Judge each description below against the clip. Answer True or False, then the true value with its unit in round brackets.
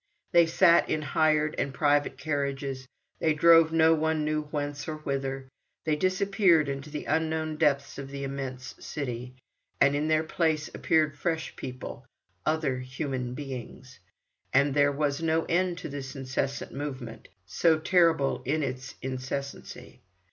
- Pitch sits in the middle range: True (145 Hz)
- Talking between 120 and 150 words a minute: True (145 wpm)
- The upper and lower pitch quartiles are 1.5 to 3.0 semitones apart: True (2.7 semitones)